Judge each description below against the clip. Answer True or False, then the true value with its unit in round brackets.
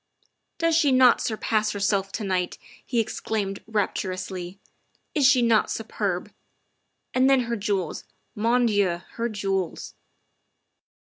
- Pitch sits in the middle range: False (210 Hz)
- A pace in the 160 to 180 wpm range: False (135 wpm)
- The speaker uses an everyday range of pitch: True (3.5 semitones)